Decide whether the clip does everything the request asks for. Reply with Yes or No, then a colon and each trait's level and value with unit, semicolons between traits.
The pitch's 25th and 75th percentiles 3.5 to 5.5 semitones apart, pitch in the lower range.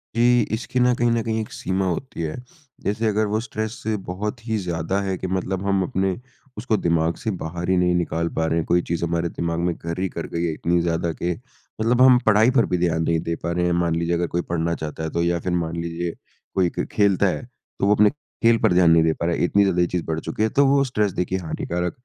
Yes: average, 4.0 semitones; very low, 90 Hz